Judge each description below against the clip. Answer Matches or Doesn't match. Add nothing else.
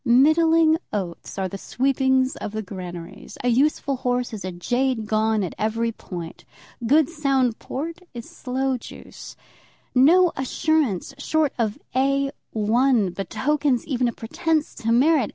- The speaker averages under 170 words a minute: Matches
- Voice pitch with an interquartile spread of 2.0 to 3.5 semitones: Doesn't match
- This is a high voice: Matches